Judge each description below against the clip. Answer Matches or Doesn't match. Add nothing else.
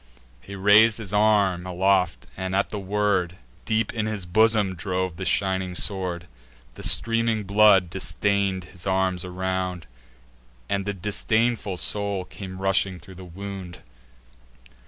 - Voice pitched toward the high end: Doesn't match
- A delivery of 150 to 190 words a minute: Doesn't match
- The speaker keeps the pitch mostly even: Matches